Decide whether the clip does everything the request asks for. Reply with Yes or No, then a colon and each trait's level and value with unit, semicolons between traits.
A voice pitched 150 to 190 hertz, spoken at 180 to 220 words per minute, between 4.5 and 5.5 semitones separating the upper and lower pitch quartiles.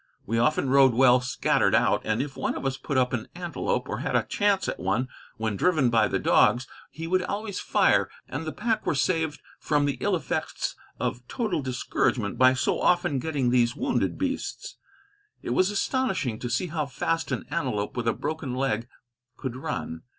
No: low, 135 Hz; average, 190 wpm; average, 5.2 semitones